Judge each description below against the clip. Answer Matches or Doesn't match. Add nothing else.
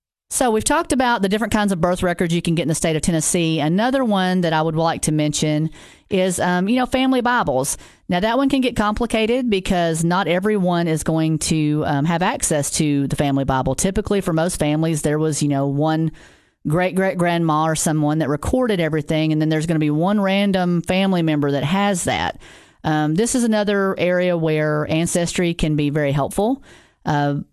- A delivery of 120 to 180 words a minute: Doesn't match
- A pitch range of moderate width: Matches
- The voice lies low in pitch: Doesn't match